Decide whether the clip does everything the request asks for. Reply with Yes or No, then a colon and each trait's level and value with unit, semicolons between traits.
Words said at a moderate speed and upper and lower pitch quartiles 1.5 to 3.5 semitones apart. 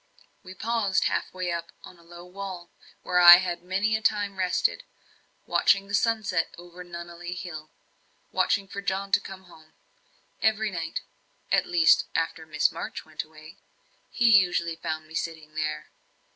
Yes: average, 160 wpm; average, 3.0 semitones